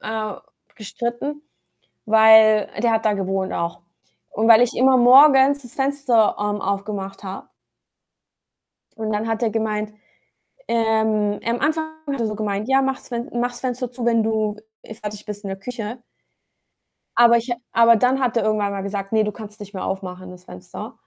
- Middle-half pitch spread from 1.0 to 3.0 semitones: Yes, average, 2.7 semitones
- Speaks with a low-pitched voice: No, high, 220 Hz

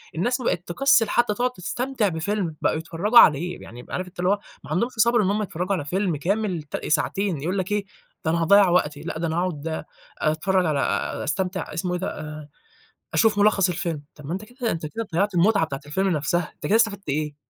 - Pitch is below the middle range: No, medium, 180 Hz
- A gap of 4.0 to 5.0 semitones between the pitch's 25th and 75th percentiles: Yes, average, 4.5 semitones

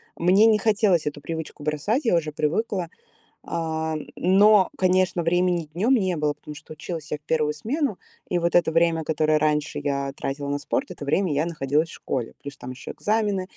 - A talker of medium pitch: Yes, medium, 165 Hz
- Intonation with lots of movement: No, average, 3.7 semitones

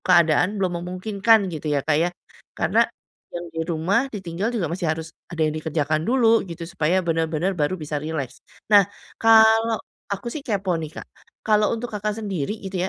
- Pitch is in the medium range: Yes, medium, 180 Hz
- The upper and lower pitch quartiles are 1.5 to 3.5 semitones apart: No, average, 4.7 semitones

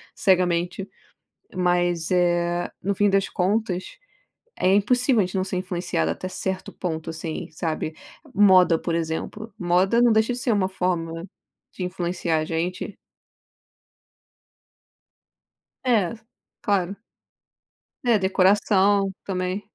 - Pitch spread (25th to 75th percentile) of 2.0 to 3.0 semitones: Yes, narrow, 2.4 semitones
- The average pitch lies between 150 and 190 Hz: Yes, medium, 185 Hz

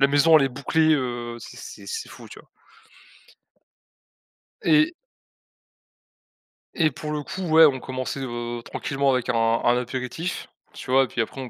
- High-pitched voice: No, low, 135 Hz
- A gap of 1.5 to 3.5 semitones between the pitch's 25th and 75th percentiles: No, average, 4.1 semitones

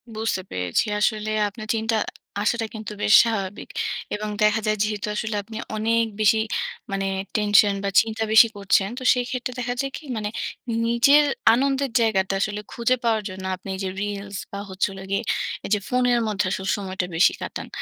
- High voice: Yes, high, 215 Hz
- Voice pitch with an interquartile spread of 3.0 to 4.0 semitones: No, narrow, 2.6 semitones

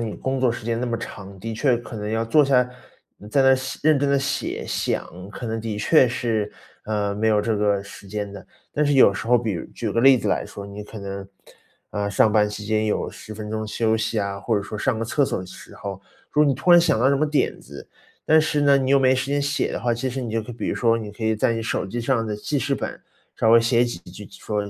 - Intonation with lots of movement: No, average, 3.9 semitones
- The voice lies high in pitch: No, low, 115 Hz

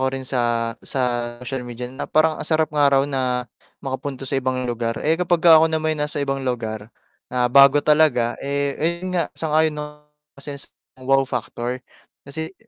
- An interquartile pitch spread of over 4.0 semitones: No, average, 3.6 semitones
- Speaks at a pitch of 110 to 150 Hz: Yes, medium, 140 Hz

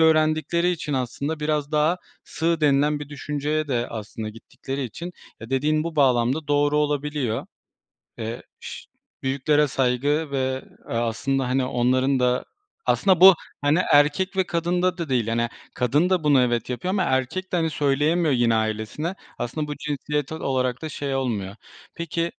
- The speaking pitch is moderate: Yes, medium, 145 Hz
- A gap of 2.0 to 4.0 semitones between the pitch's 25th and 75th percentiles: Yes, average, 3.6 semitones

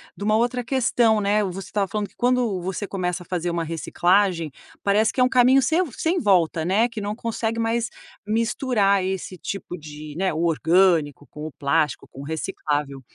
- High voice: Yes, high, 195 Hz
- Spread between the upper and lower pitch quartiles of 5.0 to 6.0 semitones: Yes, average, 5.3 semitones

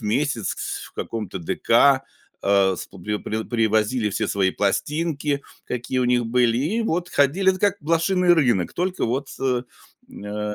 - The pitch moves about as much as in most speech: No, wide, 7.0 semitones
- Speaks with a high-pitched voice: No, low, 125 Hz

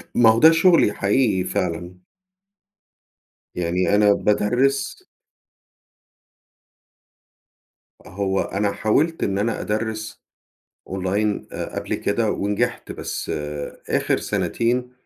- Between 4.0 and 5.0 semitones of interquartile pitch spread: No, average, 3.2 semitones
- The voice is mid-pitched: No, low, 105 Hz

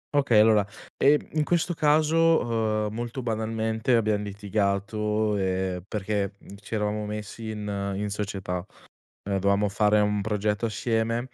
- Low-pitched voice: Yes, low, 105 Hz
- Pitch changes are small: Yes, narrow, 2.1 semitones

